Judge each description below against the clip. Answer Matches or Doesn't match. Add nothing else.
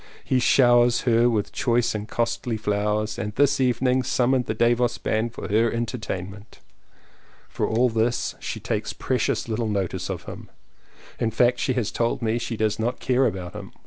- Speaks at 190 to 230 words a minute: Doesn't match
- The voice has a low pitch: Matches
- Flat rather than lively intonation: Matches